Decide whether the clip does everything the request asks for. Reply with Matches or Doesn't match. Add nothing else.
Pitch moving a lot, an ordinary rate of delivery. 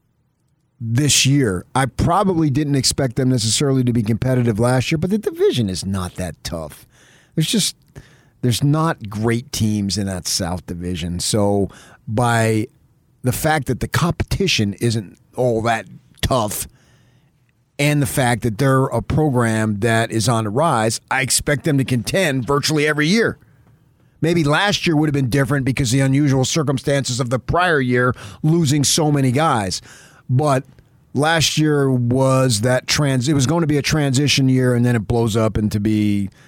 Doesn't match